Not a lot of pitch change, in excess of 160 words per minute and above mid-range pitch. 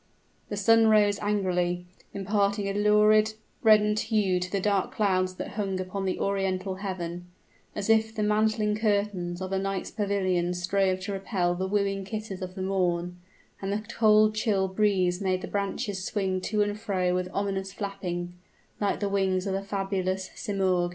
Yes: narrow, 2.0 semitones; average, 170 wpm; high, 195 Hz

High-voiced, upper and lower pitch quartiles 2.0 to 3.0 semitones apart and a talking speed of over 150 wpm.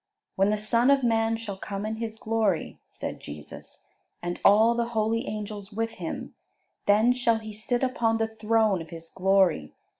Yes: high, 220 Hz; narrow, 2.4 semitones; average, 175 wpm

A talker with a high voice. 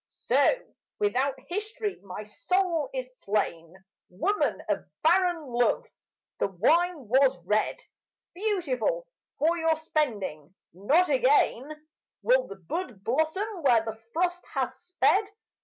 Yes: very high, 300 Hz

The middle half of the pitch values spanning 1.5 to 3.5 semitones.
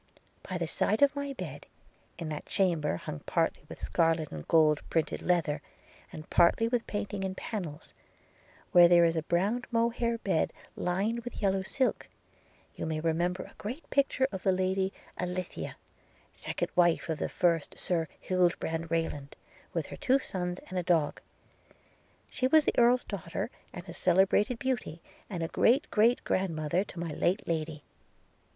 No: average, 4.5 semitones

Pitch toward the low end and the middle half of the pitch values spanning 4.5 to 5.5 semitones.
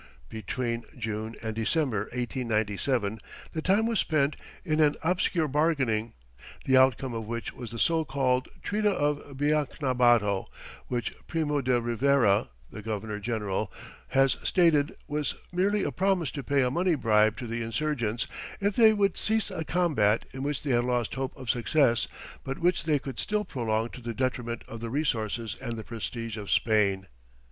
Yes: low, 125 Hz; average, 5.1 semitones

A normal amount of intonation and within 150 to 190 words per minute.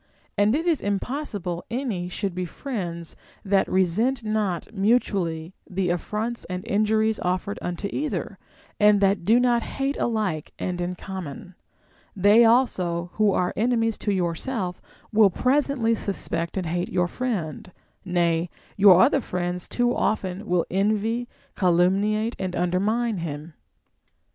No: average, 4.1 semitones; slow, 135 wpm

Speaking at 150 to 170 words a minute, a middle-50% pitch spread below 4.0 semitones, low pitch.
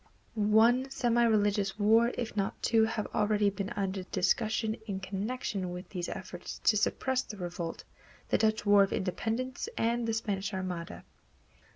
No: average, 155 wpm; average, 2.8 semitones; high, 210 Hz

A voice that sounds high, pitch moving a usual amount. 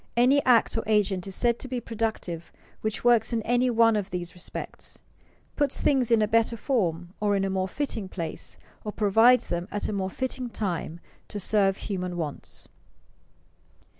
Yes: high, 215 Hz; average, 4.0 semitones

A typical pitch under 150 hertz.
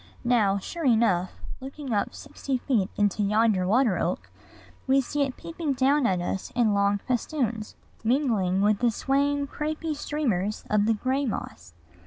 No: high, 235 Hz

